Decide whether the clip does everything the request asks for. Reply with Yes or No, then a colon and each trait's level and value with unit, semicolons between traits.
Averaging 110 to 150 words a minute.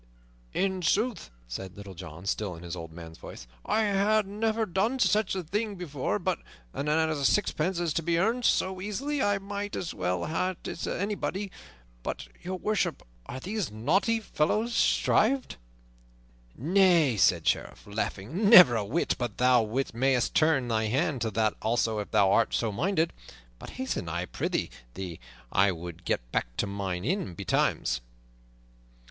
No: average, 165 wpm